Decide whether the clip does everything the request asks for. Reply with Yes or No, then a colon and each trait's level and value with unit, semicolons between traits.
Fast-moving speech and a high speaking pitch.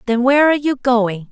Yes: fast, 230 wpm; very high, 250 Hz